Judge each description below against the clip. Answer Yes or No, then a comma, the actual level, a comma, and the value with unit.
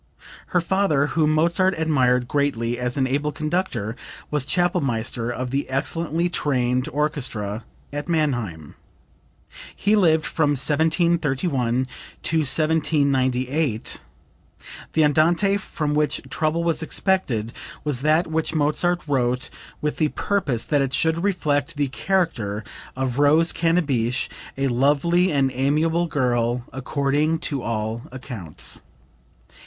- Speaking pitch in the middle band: Yes, medium, 145 Hz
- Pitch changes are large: No, average, 4.2 semitones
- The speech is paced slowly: Yes, slow, 115 wpm